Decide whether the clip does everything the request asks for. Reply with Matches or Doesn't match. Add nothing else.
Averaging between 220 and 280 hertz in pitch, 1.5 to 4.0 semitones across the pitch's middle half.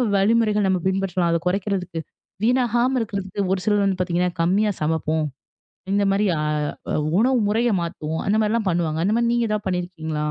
Doesn't match